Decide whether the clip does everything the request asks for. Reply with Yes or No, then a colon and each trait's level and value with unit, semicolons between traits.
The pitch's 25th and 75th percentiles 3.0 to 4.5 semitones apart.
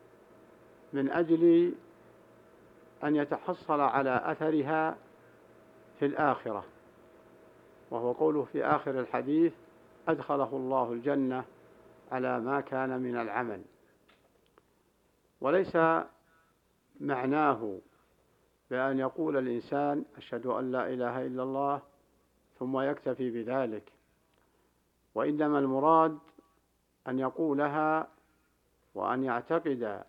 Yes: average, 3.5 semitones